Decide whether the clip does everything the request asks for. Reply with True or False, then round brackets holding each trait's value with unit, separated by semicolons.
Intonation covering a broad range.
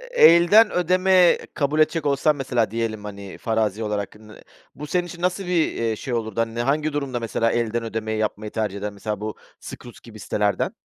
True (6.2 semitones)